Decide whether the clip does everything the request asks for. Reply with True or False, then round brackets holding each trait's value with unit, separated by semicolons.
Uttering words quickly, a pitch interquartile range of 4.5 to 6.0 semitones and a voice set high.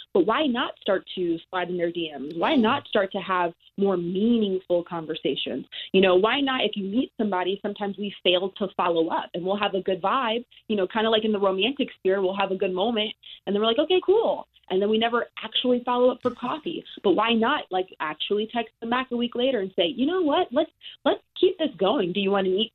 True (245 wpm; 4.8 semitones; 205 Hz)